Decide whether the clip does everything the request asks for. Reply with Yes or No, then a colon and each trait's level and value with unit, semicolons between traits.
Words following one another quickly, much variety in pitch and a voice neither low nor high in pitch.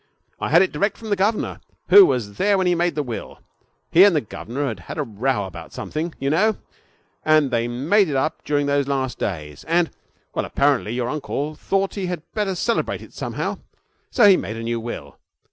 Yes: fast, 210 wpm; wide, 7.3 semitones; medium, 150 Hz